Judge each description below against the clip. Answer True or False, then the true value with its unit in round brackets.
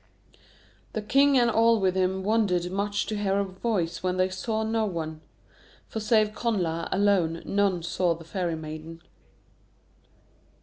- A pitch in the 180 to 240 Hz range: True (190 Hz)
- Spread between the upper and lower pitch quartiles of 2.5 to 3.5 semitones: False (3.9 semitones)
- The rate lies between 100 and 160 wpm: True (145 wpm)